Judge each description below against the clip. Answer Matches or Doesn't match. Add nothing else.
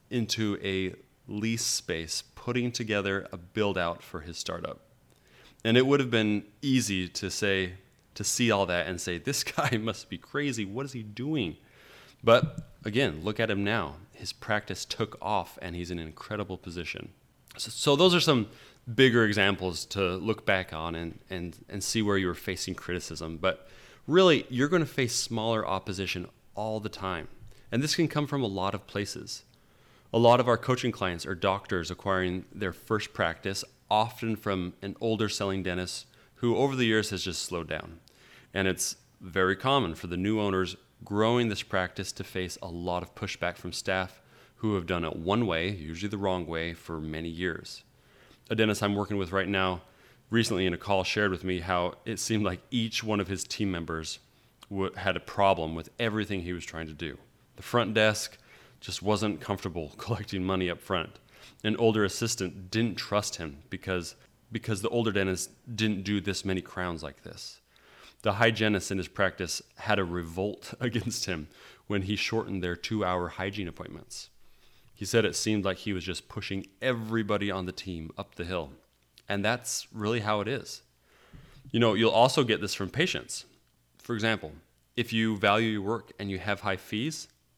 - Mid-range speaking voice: Doesn't match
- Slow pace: Doesn't match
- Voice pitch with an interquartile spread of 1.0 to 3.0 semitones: Doesn't match